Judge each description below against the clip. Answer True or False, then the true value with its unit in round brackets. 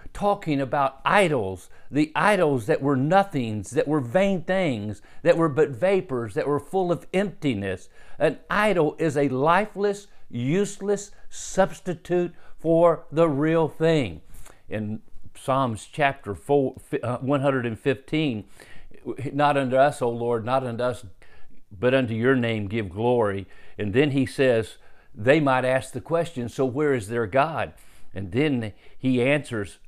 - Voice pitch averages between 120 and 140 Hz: True (135 Hz)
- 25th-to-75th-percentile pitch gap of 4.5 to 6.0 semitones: True (5.3 semitones)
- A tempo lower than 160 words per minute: True (135 wpm)